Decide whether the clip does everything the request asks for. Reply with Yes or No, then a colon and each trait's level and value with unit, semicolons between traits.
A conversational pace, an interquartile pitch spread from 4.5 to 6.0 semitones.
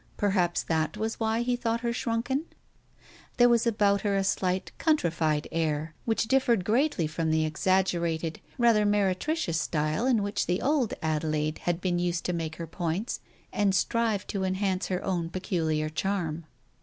Yes: average, 160 wpm; wide, 5.4 semitones